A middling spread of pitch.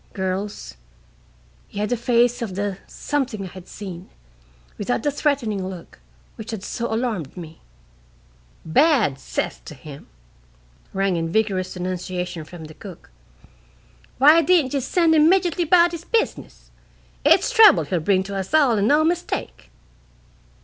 No: wide, 7.9 semitones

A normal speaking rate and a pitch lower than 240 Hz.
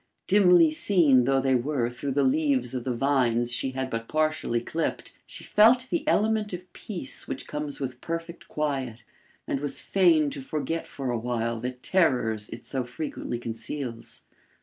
Yes: average, 165 wpm; low, 135 Hz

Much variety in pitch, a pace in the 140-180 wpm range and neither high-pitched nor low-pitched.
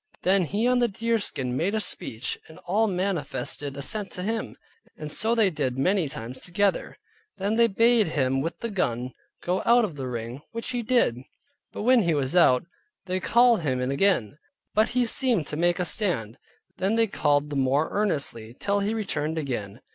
No: wide, 7.8 semitones; average, 190 wpm; medium, 180 Hz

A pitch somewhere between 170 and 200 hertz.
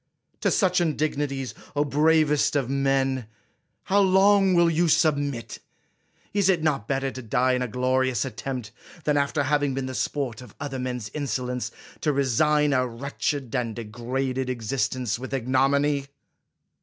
No: low, 135 Hz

